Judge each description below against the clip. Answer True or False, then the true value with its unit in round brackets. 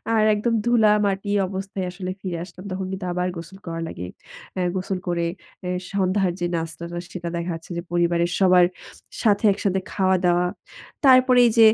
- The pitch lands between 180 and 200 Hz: True (185 Hz)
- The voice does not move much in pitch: True (2.3 semitones)